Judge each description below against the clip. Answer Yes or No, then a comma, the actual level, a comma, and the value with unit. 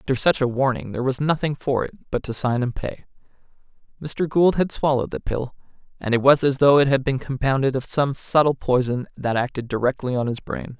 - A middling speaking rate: No, fast, 215 wpm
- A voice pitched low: Yes, low, 130 Hz